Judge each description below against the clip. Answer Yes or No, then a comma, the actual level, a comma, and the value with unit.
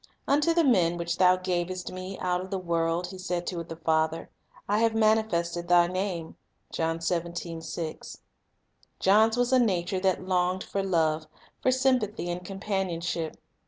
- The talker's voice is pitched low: No, medium, 185 Hz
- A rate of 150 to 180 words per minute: Yes, average, 155 wpm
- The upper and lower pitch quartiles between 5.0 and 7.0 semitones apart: No, average, 3.0 semitones